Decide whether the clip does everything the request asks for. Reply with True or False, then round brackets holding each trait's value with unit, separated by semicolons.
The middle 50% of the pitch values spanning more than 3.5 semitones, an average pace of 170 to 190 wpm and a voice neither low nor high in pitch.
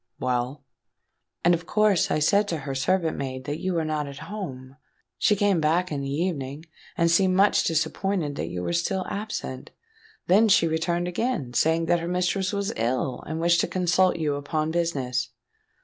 True (4.5 semitones; 180 wpm; 165 Hz)